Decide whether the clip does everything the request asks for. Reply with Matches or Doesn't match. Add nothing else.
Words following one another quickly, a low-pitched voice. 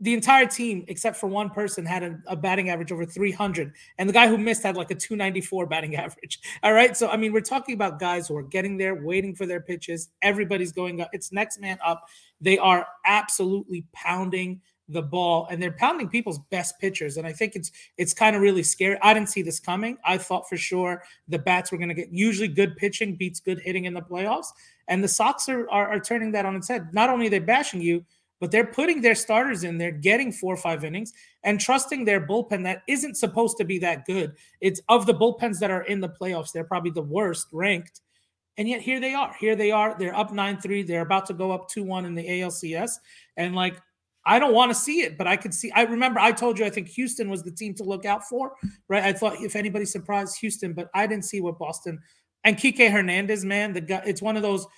Doesn't match